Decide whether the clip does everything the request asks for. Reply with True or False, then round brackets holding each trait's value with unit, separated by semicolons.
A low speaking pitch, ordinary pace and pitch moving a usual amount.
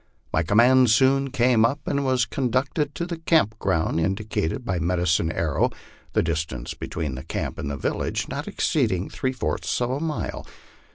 False (115 Hz; 170 wpm; 8.0 semitones)